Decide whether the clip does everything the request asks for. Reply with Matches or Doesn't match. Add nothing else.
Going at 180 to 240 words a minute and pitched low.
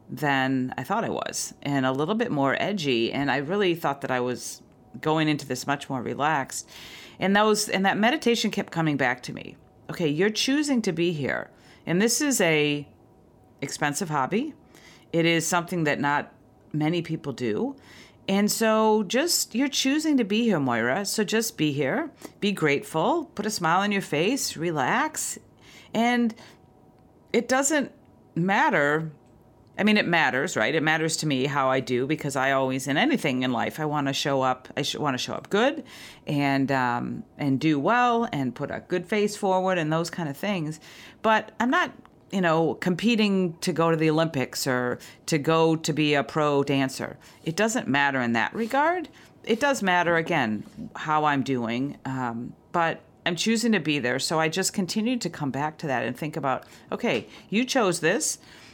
Doesn't match